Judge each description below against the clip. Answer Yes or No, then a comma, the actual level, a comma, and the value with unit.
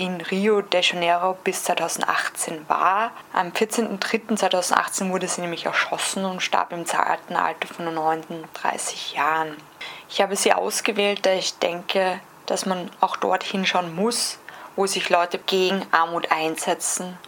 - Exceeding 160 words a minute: No, average, 140 wpm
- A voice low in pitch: No, medium, 185 Hz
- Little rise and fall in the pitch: Yes, narrow, 1.9 semitones